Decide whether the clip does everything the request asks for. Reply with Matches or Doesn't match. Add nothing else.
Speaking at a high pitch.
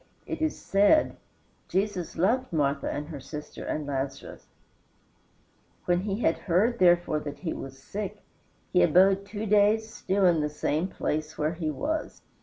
Doesn't match